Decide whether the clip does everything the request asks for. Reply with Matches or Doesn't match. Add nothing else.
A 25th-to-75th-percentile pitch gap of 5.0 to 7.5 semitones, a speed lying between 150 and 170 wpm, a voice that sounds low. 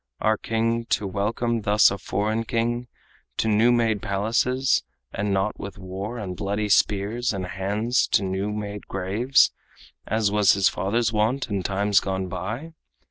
Doesn't match